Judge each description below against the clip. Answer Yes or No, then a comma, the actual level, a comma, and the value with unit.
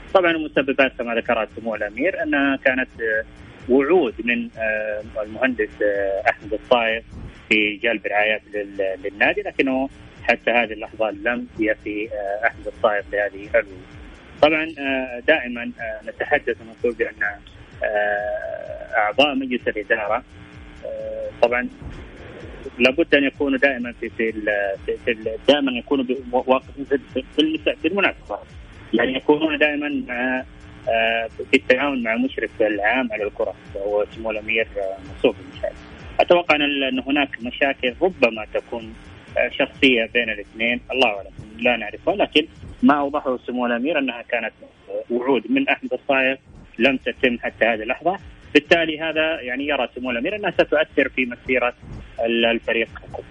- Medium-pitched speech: No, low, 125 Hz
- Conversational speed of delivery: No, slow, 110 wpm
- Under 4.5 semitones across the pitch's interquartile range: No, average, 5.2 semitones